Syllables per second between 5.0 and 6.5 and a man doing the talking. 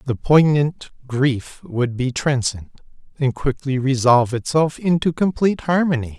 No: 4.5 syllables/s; male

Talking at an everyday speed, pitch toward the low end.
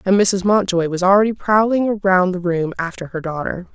No: average, 190 wpm; high, 190 Hz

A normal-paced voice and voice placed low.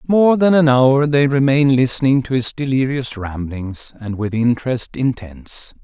Yes: average, 155 wpm; low, 130 Hz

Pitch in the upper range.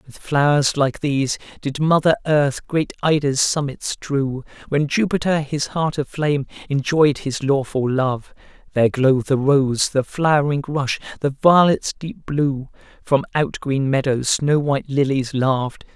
No: medium, 140 Hz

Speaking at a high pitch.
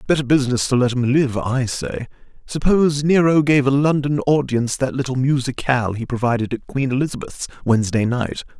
No: low, 130 Hz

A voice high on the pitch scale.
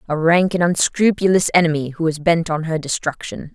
No: medium, 165 Hz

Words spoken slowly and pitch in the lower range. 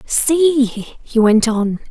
No: slow, 125 wpm; high, 245 Hz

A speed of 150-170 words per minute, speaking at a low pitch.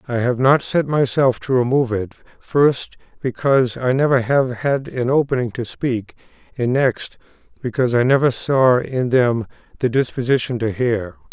Yes: average, 160 wpm; low, 125 Hz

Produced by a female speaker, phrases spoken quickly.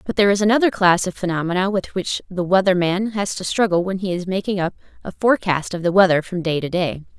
Yes: female; fast, 240 wpm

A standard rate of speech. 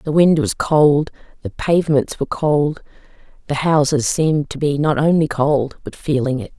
Yes: average, 175 wpm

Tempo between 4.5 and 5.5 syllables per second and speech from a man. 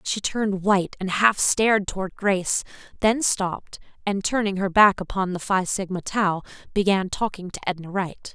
No: 5.0 syllables/s; female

